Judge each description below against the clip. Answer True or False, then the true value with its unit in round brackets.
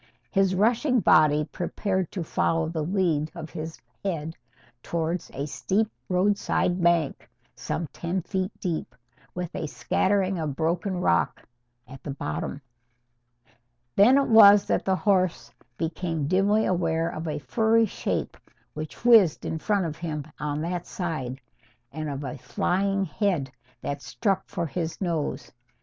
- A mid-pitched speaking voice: True (170 Hz)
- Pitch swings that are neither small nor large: True (3.9 semitones)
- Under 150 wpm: True (140 wpm)